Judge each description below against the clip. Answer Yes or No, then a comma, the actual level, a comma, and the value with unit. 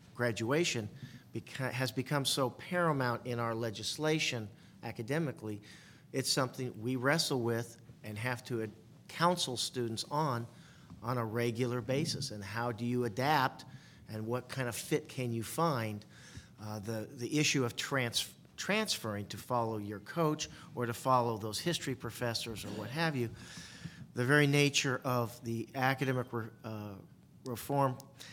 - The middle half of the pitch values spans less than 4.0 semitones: Yes, average, 3.2 semitones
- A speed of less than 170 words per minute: Yes, average, 145 wpm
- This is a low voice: Yes, low, 125 Hz